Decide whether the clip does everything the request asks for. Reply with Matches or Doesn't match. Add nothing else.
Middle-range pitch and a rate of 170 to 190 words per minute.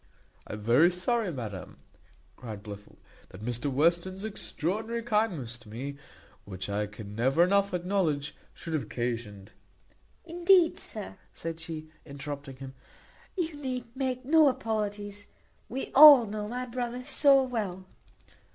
Doesn't match